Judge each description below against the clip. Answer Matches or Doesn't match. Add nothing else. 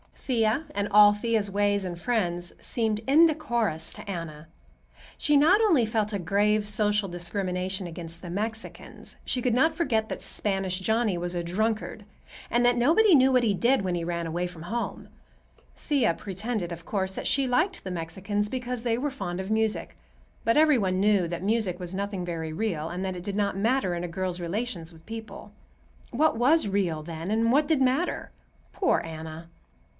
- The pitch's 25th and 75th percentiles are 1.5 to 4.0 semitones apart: Doesn't match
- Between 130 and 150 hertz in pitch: Doesn't match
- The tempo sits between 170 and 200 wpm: Matches